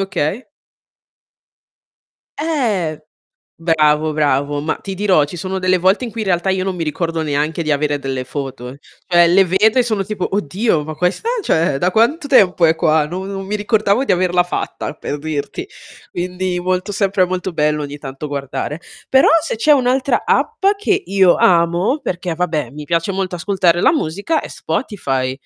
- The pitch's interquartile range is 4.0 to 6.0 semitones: Yes, average, 4.6 semitones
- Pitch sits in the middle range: Yes, medium, 180 Hz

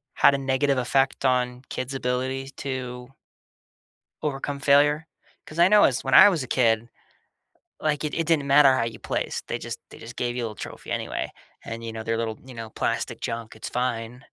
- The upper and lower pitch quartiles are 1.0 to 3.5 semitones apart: Yes, average, 2.9 semitones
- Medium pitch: No, low, 130 Hz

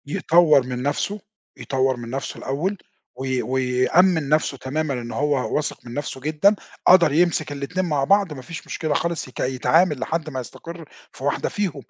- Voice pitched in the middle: Yes, medium, 145 Hz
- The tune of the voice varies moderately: Yes, average, 4.1 semitones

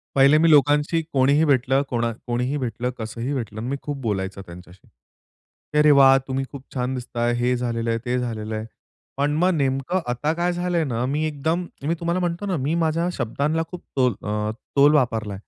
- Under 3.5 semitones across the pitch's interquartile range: No, average, 4.3 semitones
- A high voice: No, low, 135 Hz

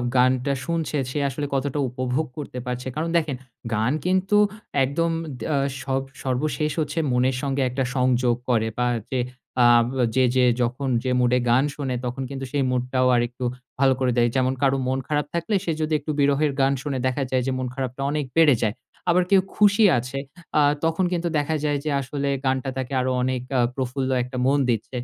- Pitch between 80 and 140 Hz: Yes, low, 135 Hz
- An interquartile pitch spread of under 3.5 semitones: Yes, average, 2.7 semitones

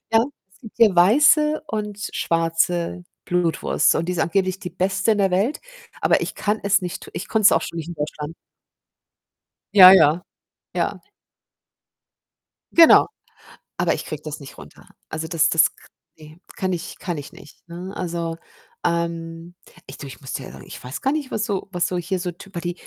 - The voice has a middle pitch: Yes, medium, 175 Hz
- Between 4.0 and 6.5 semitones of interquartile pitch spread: No, average, 3.0 semitones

